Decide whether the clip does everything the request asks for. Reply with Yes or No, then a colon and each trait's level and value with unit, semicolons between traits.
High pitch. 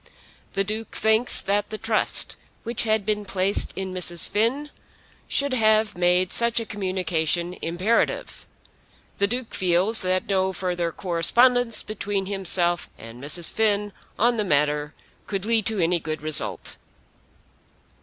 Yes: high, 195 Hz